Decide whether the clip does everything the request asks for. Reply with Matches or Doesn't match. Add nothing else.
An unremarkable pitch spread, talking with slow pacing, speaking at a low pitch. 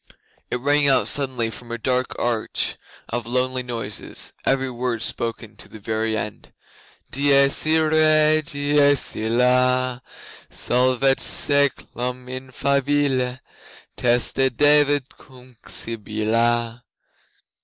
Matches